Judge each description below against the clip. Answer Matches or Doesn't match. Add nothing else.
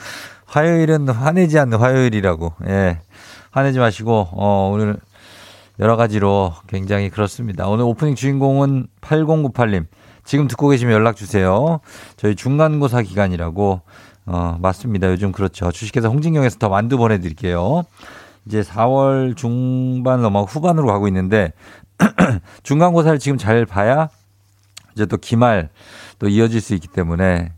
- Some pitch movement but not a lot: Matches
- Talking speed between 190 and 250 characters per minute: Doesn't match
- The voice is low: Matches